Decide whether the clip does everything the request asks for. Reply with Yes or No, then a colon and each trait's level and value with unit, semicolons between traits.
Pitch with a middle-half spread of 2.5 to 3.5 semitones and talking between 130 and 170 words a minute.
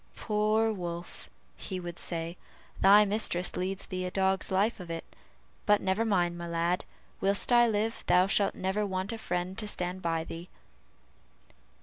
Yes: average, 2.9 semitones; average, 160 wpm